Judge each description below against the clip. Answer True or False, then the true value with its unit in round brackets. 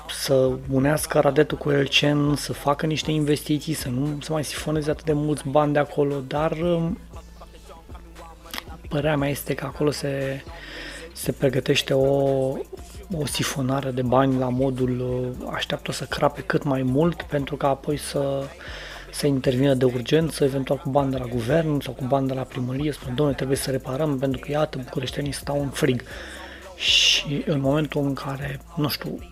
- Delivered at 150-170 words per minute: True (165 wpm)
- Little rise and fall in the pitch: True (1.9 semitones)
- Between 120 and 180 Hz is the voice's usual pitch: True (140 Hz)